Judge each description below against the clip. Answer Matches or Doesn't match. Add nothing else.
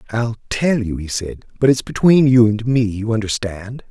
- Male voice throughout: Matches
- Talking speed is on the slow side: Doesn't match